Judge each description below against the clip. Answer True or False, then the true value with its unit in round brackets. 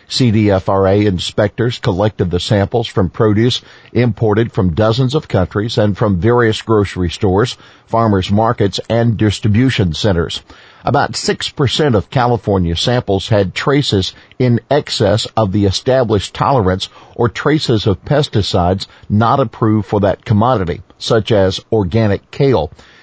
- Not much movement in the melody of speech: False (3.3 semitones)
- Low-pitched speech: True (110 Hz)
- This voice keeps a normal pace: False (125 wpm)